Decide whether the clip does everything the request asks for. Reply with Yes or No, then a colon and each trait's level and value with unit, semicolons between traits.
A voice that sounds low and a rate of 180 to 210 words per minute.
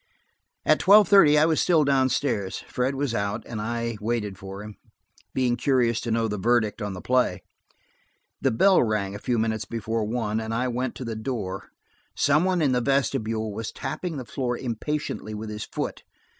Yes: low, 115 Hz; average, 185 wpm